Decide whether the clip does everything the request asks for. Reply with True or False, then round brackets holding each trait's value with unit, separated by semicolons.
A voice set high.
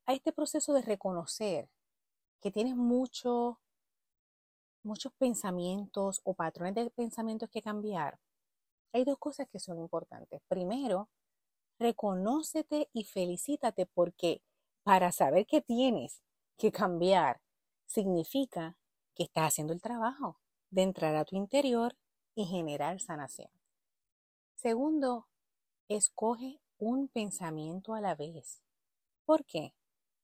True (215 Hz)